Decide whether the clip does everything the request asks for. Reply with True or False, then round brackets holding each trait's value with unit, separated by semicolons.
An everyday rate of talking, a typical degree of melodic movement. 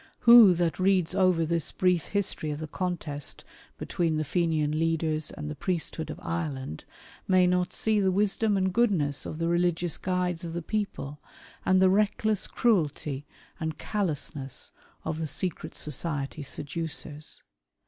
True (150 wpm; 3.4 semitones)